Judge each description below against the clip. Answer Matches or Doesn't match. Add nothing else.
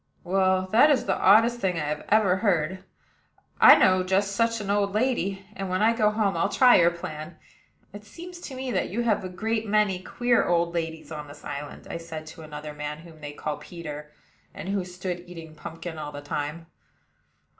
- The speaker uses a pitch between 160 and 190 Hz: Matches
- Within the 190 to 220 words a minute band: Matches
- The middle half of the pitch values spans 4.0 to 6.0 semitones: Matches